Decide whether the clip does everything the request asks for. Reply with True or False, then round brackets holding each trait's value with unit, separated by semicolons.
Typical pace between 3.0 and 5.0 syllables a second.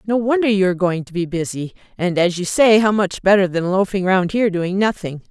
False (5.7 syllables/s)